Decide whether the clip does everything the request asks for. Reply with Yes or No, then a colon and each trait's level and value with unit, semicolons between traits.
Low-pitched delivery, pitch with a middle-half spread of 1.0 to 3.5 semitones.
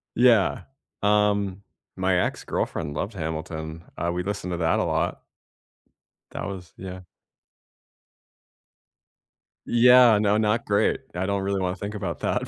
Yes: very low, 95 Hz; average, 2.7 semitones